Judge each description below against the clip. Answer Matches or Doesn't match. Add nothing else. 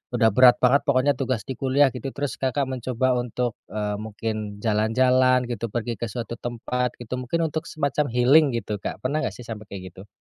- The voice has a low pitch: Matches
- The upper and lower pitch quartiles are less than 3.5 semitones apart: Matches